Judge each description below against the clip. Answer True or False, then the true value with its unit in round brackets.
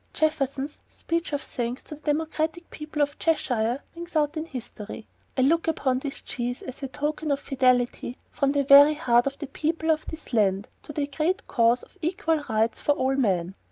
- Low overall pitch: False (280 Hz)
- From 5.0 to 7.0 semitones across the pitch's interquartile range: False (3.9 semitones)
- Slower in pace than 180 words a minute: False (195 wpm)